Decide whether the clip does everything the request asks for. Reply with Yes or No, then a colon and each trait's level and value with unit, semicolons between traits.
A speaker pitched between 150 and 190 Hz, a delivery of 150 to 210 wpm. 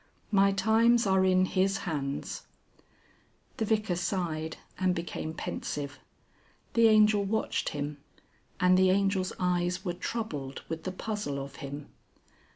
No: medium, 185 Hz; slow, 135 wpm